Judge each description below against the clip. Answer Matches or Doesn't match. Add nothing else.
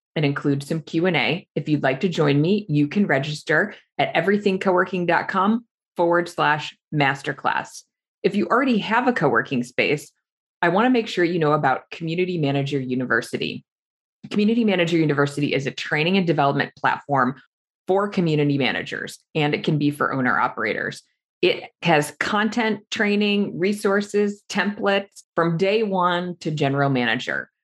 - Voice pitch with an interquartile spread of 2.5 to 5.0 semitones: Doesn't match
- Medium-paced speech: Matches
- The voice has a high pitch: Doesn't match